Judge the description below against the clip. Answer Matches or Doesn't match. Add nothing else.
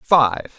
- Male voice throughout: Matches